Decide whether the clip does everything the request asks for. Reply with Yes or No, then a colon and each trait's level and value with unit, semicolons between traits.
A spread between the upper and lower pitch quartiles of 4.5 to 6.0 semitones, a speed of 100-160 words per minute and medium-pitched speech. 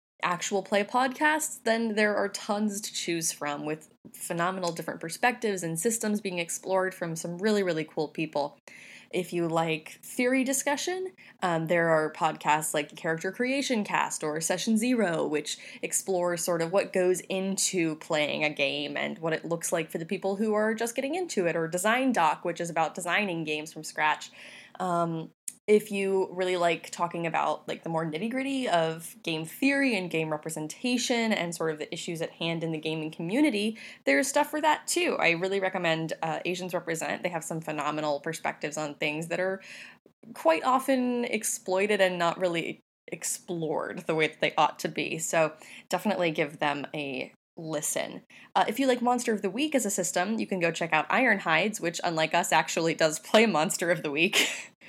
No: average, 5.0 semitones; average, 185 wpm; medium, 175 Hz